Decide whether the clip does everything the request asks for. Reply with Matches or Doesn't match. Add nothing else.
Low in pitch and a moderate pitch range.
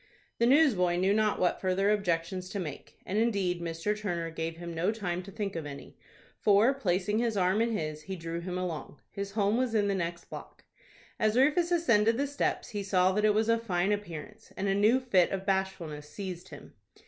Doesn't match